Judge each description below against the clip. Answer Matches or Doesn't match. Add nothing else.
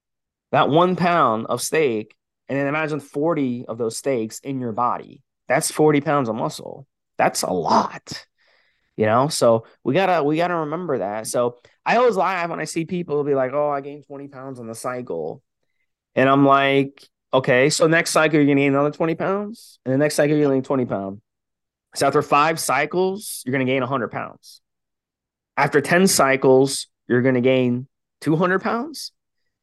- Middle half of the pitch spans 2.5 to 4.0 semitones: Matches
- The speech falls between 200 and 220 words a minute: Doesn't match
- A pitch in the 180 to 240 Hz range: Doesn't match